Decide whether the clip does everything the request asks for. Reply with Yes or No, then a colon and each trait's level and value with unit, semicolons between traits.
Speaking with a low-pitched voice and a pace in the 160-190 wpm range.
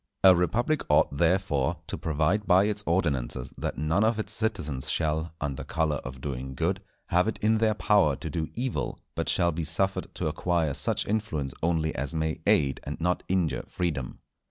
Yes: very low, 80 Hz; average, 180 wpm